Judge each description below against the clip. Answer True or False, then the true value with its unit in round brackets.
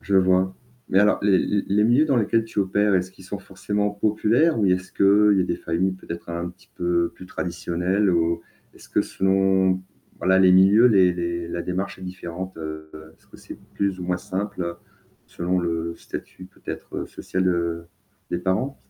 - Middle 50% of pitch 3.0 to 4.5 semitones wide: False (2.4 semitones)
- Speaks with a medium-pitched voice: False (95 Hz)